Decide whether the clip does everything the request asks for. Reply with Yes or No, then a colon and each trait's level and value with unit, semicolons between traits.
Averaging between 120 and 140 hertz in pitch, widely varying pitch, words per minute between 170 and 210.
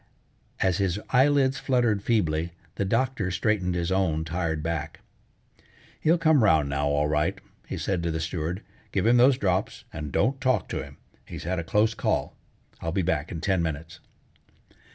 No: very low, 90 Hz; wide, 5.9 semitones; average, 175 wpm